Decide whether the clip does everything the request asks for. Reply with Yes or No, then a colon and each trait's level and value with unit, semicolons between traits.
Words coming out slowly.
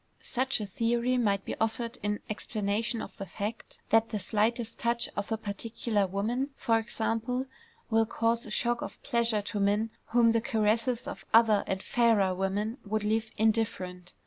No: average, 170 wpm